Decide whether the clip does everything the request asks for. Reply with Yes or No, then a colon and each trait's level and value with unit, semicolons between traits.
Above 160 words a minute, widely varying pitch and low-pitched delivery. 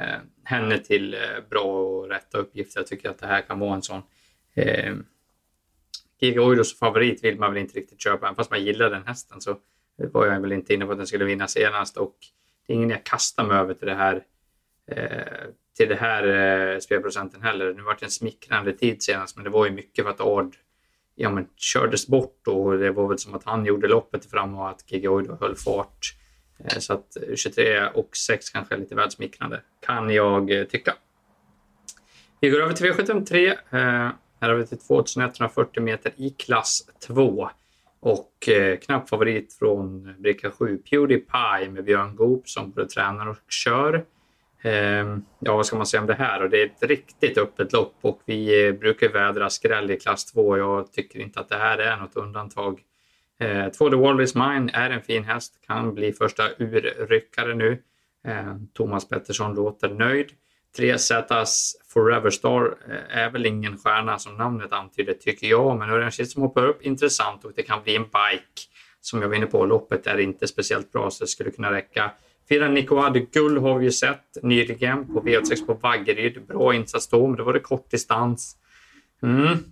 Yes: average, 190 wpm; wide, 5.9 semitones; low, 115 Hz